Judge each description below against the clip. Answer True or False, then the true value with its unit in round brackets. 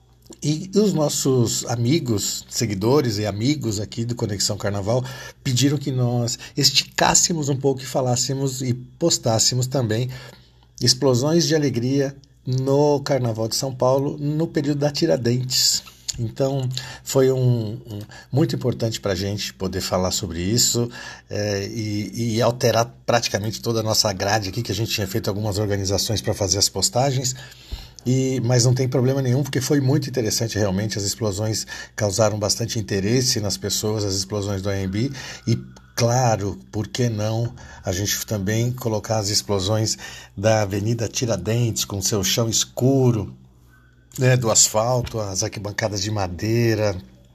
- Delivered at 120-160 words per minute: True (145 wpm)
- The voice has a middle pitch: False (115 Hz)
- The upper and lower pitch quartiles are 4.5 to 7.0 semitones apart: False (4.0 semitones)